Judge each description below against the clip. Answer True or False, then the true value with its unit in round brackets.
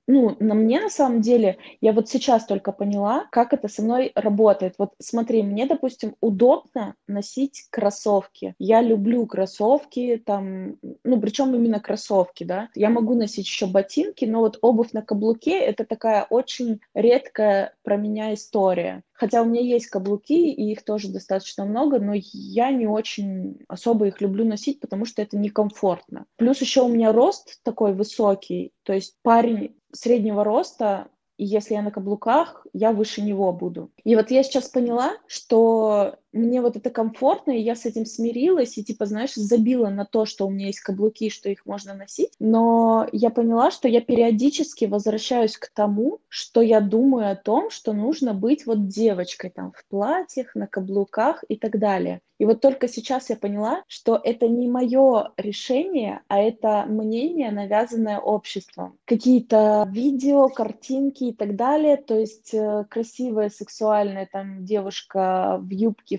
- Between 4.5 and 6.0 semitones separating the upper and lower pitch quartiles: False (3.1 semitones)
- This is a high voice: True (225 Hz)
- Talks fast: True (165 wpm)